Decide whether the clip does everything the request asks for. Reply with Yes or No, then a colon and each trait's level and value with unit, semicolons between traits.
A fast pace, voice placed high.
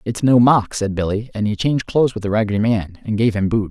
No: fast, 275 wpm; low, 110 Hz